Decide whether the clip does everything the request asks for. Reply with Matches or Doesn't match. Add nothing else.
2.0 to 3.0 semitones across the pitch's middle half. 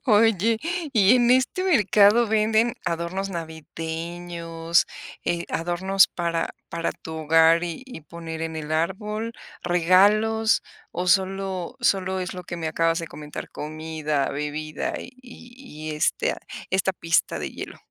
Doesn't match